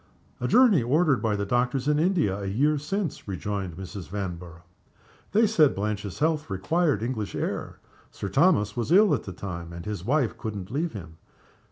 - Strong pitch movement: Yes, wide, 7.7 semitones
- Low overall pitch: Yes, low, 110 Hz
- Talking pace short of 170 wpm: No, average, 175 wpm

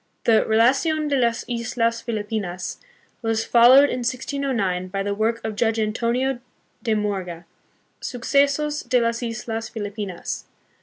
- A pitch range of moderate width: Yes, average, 3.0 semitones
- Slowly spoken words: Yes, slow, 125 wpm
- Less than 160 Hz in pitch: No, high, 230 Hz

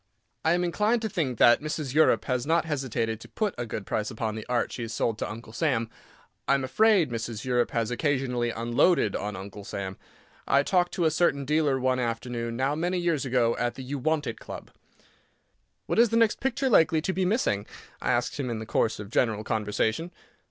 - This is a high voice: No, low, 130 Hz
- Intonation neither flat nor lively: No, wide, 5.9 semitones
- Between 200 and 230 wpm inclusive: Yes, fast, 205 wpm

